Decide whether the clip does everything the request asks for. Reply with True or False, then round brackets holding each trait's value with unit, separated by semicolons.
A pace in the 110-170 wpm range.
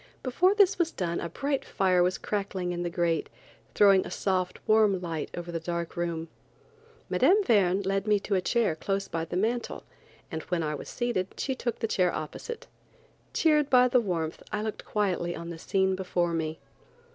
False (190 wpm)